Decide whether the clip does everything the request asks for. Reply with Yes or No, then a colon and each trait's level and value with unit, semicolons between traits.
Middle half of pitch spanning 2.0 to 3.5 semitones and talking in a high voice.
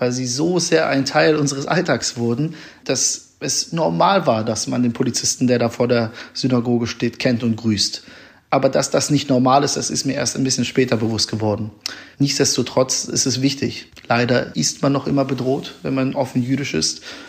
No: average, 2.7 semitones; low, 125 Hz